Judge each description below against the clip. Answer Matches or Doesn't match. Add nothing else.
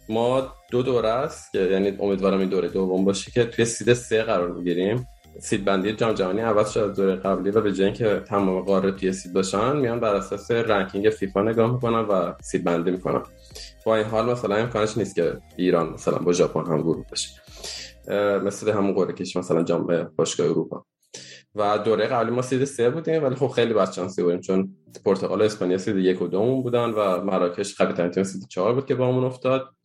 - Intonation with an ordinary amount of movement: Matches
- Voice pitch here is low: Matches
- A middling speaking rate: Doesn't match